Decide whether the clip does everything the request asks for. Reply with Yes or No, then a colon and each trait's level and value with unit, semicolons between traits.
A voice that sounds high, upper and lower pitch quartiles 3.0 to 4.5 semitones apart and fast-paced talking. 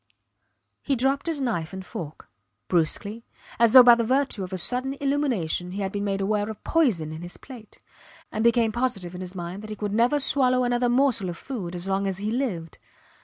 No: high, 215 Hz; wide, 5.4 semitones; fast, 210 wpm